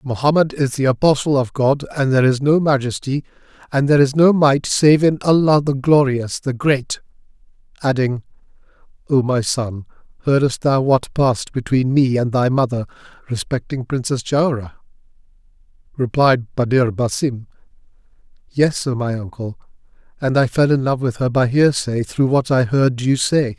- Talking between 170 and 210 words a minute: No, average, 155 wpm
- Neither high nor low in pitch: No, low, 130 Hz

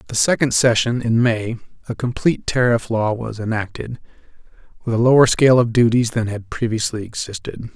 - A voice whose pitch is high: No, low, 115 Hz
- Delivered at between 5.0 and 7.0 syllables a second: Yes, 5.5 syllables/s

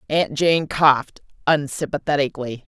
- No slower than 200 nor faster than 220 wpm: No, slow, 85 wpm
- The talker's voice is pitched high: No, medium, 145 Hz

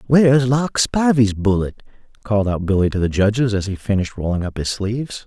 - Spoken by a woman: No, male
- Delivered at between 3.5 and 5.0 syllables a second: No, 5.8 syllables/s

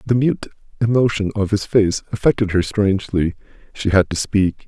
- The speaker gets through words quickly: No, average, 165 wpm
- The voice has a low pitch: Yes, low, 100 Hz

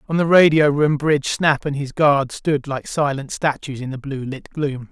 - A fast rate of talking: Yes, fast, 220 wpm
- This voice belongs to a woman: No, male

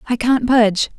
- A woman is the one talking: Yes, female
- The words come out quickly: No, average, 185 wpm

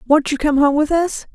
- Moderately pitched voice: No, very high, 295 Hz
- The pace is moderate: No, fast, 265 wpm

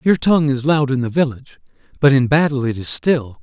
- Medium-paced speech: No, fast, 230 wpm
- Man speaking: Yes, male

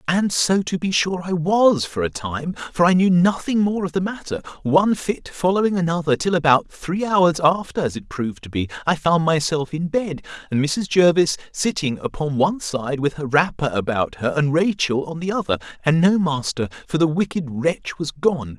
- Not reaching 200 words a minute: No, fast, 205 wpm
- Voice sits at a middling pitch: Yes, medium, 160 Hz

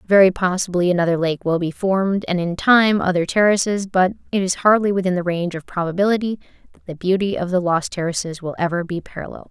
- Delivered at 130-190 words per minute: No, average, 200 wpm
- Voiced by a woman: Yes, female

